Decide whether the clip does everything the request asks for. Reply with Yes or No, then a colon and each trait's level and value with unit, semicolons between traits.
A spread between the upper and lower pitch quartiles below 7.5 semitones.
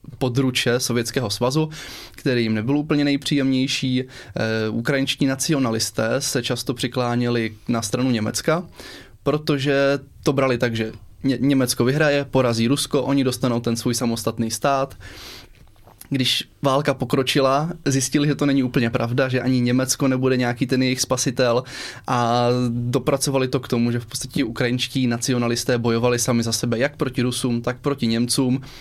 Yes: narrow, 2.4 semitones